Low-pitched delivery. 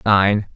Yes: low, 100 Hz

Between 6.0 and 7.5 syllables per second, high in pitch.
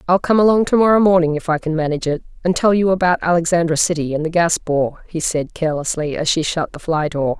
No: 6.2 syllables/s; medium, 165 Hz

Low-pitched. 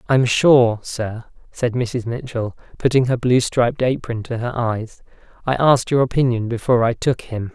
Yes: low, 120 Hz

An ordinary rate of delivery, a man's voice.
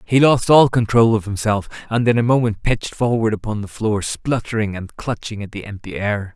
No: fast, 210 wpm; male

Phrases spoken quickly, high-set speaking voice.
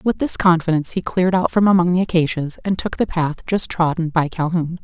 No: fast, 225 wpm; medium, 170 Hz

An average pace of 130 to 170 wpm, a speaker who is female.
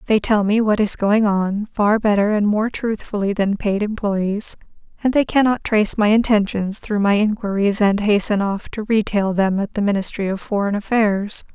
No: average, 185 wpm; female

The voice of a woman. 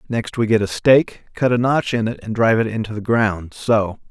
No: male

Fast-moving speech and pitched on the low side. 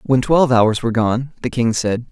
Yes: fast, 225 wpm; low, 125 Hz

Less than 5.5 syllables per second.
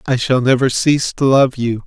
Yes: 5.1 syllables/s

